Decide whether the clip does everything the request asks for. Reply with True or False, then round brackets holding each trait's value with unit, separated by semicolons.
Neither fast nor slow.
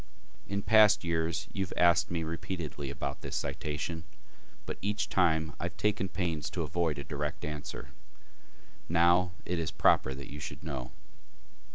True (160 wpm)